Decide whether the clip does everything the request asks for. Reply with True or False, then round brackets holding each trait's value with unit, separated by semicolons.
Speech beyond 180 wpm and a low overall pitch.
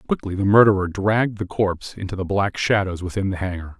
True (205 wpm; 95 Hz)